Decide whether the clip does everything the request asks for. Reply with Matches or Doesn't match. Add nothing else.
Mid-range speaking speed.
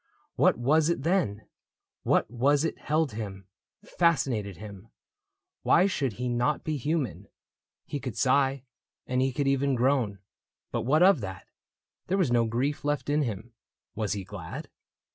Matches